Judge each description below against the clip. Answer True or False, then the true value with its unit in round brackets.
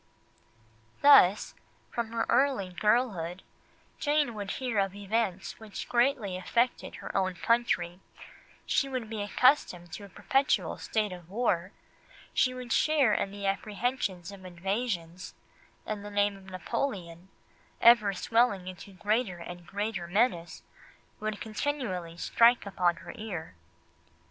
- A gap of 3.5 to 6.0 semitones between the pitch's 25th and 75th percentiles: True (4.5 semitones)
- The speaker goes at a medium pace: False (130 wpm)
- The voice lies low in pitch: False (205 Hz)